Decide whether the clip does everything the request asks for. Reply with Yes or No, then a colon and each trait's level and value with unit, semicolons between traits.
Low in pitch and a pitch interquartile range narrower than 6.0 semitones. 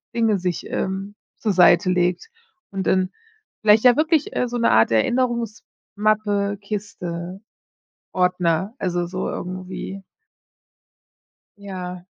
No: high, 195 Hz; average, 2.9 semitones